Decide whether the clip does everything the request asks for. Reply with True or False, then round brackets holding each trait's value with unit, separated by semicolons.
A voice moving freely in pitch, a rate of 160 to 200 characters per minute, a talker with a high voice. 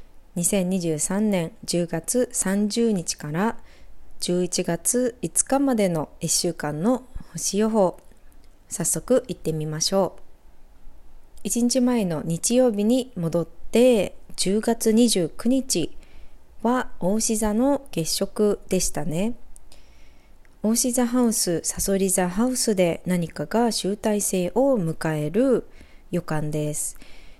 True (5.8 semitones; 170 characters per minute; 195 Hz)